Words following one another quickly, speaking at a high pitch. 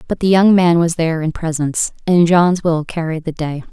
No: fast, 225 wpm; medium, 165 Hz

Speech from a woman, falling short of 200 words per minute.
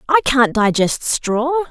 Yes: female; average, 140 wpm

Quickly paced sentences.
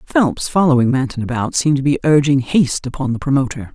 No: average, 190 wpm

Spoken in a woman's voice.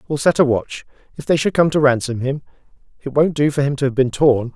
No: male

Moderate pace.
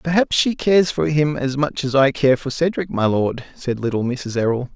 No: fast, 225 wpm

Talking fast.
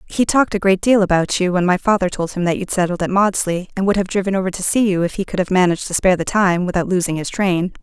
Yes: fast, 290 wpm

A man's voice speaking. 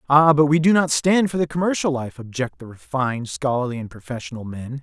Yes: male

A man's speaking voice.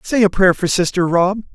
Yes: male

